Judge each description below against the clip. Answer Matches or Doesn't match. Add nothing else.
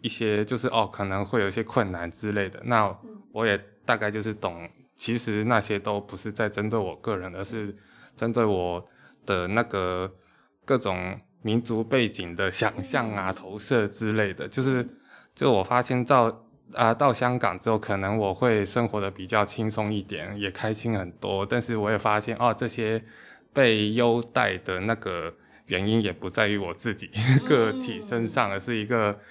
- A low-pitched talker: Matches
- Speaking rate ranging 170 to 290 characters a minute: Matches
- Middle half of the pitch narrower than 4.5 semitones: Matches